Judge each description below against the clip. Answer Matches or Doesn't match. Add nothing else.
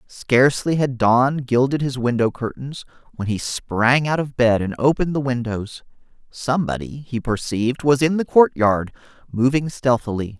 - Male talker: Matches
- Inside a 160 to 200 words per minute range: Doesn't match